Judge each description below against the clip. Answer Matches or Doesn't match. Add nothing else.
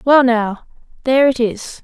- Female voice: Matches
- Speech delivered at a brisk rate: Doesn't match